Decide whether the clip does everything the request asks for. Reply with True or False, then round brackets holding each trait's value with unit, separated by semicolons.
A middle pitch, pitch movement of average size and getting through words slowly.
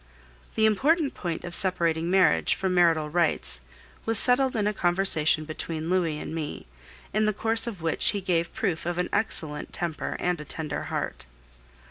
False (175 Hz; 4.4 semitones; 170 wpm)